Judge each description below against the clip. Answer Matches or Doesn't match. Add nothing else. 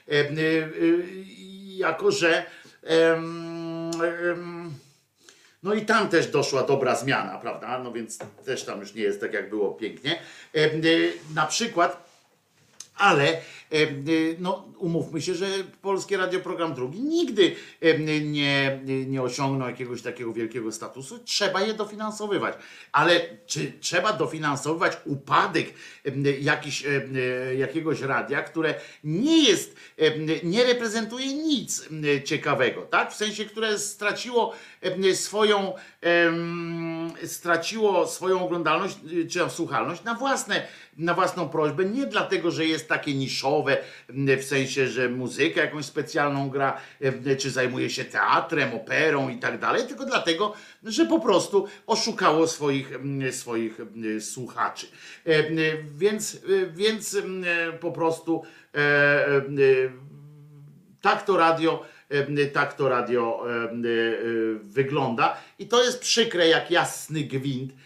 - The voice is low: Doesn't match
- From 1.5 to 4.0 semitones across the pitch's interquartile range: Doesn't match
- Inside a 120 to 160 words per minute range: Doesn't match